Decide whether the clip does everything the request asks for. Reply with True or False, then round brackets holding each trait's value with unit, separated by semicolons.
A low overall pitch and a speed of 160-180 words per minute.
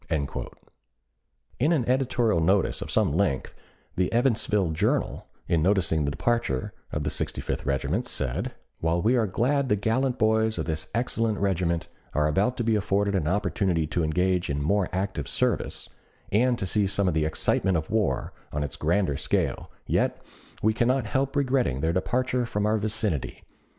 True (100 Hz; 170 wpm)